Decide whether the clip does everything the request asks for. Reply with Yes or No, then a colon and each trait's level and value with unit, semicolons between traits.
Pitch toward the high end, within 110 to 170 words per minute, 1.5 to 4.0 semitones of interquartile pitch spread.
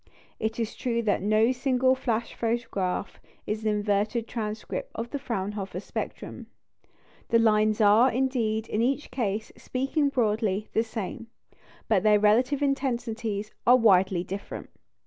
Yes: high, 225 Hz; slow, 135 wpm; average, 2.9 semitones